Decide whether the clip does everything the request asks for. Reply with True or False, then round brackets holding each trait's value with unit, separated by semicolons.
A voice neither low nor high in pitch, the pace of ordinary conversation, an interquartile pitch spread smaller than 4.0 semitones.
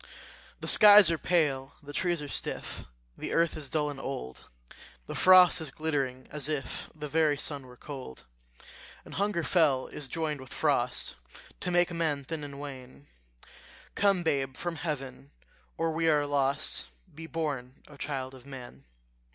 True (145 Hz; 160 wpm; 3.3 semitones)